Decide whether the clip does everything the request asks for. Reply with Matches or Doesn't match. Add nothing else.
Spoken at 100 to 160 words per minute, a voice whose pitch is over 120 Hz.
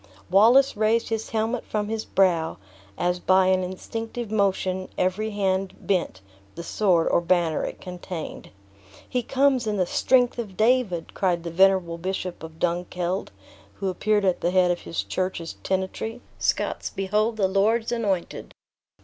Matches